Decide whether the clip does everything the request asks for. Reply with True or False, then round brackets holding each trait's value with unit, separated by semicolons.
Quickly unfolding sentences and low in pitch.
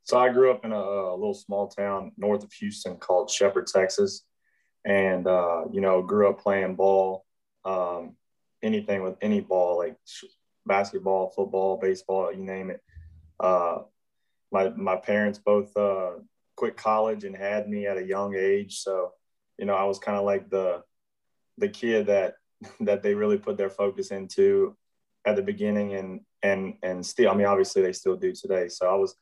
False (180 wpm; 100 Hz)